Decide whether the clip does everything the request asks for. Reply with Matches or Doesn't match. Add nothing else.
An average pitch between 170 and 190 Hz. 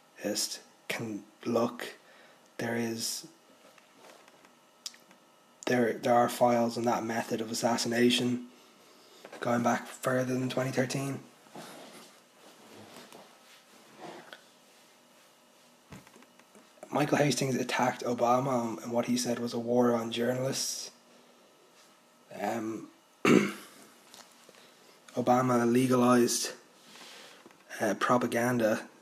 Doesn't match